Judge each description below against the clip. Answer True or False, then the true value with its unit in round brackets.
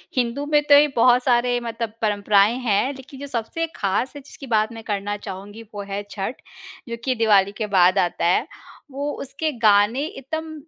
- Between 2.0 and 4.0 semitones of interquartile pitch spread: False (4.6 semitones)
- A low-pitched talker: False (230 Hz)